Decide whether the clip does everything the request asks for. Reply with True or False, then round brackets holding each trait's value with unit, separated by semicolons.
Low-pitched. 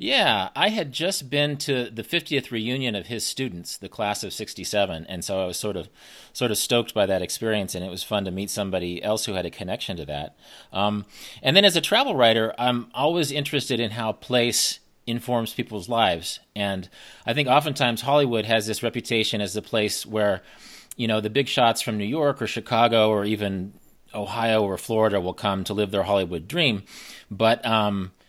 True (110 Hz)